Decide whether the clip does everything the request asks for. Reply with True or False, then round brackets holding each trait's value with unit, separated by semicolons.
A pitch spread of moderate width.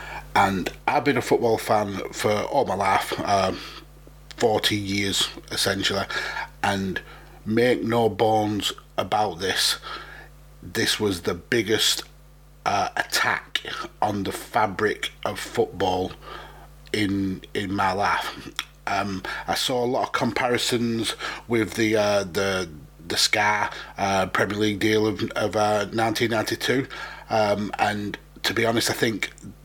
False (1.9 semitones)